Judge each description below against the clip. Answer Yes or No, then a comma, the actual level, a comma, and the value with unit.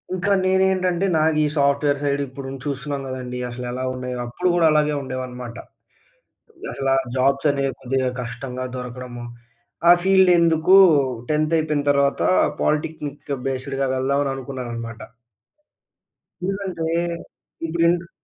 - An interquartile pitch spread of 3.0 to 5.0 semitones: Yes, average, 3.7 semitones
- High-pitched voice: No, medium, 140 Hz